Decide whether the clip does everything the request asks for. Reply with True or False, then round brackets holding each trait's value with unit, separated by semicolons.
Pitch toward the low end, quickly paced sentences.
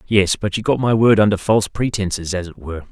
True (100 Hz; 245 wpm)